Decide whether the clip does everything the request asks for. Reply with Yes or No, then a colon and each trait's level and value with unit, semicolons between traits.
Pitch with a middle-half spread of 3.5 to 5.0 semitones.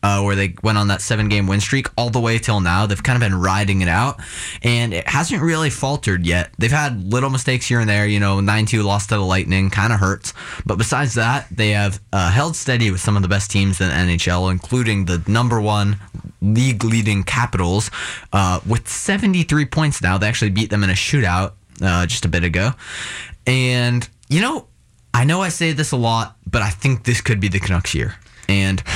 Yes: average, 3.9 semitones